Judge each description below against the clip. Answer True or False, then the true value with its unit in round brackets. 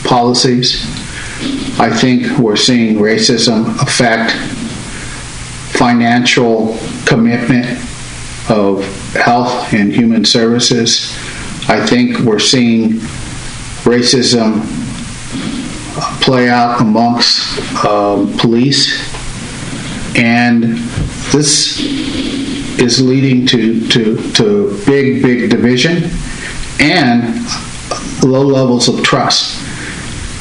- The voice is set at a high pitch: False (120 Hz)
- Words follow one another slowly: True (75 wpm)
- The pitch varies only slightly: True (2.2 semitones)